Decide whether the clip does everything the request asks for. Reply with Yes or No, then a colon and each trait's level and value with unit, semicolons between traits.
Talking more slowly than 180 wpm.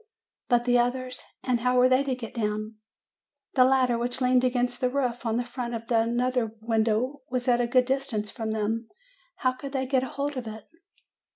No: average, 195 wpm